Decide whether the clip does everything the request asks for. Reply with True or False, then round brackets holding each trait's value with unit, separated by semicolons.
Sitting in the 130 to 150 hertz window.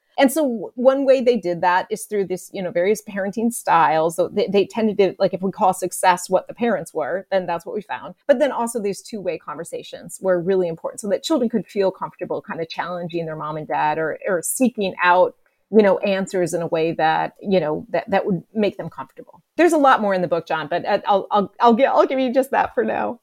False (195 Hz)